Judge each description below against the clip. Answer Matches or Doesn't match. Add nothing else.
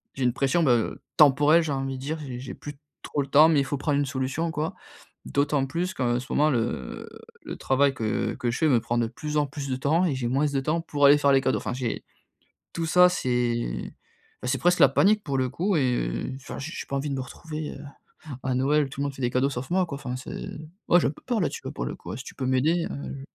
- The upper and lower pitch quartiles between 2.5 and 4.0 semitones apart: Matches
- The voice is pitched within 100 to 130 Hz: Doesn't match